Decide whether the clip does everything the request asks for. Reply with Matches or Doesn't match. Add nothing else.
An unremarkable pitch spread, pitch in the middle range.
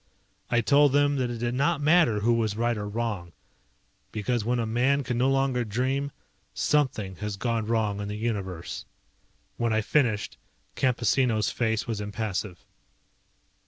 Doesn't match